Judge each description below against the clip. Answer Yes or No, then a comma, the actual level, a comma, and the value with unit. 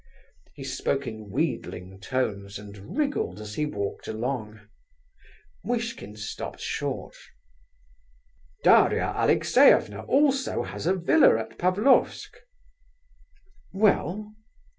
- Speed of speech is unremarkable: No, slow, 95 wpm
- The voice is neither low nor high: No, low, 130 Hz